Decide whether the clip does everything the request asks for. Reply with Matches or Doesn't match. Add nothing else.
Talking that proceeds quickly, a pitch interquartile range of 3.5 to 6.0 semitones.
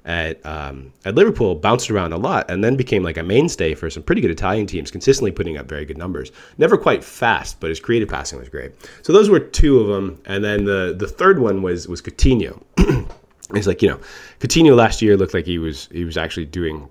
Matches